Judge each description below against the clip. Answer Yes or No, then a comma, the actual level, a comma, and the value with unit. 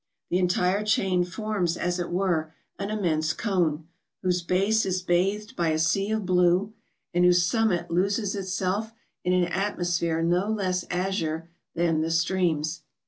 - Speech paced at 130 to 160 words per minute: Yes, average, 150 wpm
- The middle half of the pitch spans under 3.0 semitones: Yes, narrow, 2.4 semitones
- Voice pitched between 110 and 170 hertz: No, medium, 180 Hz